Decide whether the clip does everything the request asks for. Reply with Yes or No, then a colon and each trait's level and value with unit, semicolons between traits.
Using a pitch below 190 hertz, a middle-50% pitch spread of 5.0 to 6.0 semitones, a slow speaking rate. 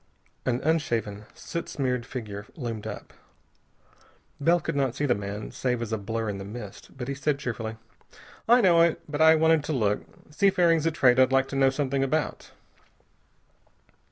No: low, 135 Hz; wide, 5.5 semitones; average, 175 wpm